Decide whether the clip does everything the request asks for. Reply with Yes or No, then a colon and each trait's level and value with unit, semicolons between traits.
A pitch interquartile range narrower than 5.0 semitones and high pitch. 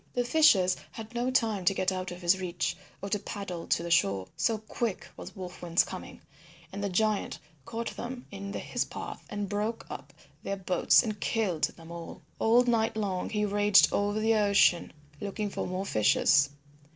Yes: average, 3.3 semitones; high, 200 Hz